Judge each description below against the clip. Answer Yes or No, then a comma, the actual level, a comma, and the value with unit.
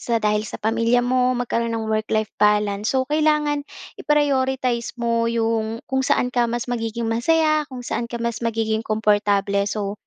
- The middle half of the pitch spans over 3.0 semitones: No, narrow, 2.6 semitones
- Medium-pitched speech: No, high, 230 Hz